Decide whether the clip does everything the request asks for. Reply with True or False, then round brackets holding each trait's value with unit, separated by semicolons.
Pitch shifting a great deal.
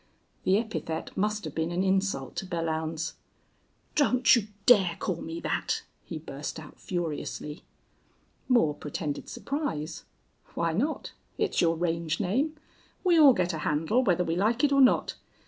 True (6.2 semitones)